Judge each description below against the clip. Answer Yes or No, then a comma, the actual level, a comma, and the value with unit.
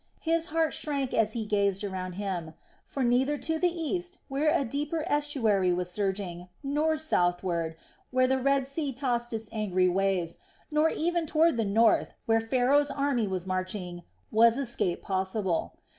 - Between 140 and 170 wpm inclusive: Yes, average, 160 wpm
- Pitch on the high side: Yes, high, 235 Hz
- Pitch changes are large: Yes, wide, 7.4 semitones